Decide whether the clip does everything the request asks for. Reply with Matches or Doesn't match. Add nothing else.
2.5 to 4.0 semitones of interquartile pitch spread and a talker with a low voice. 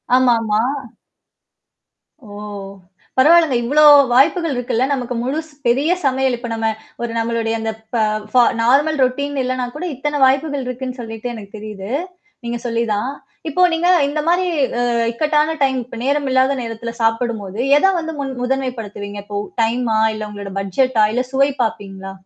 Doesn't match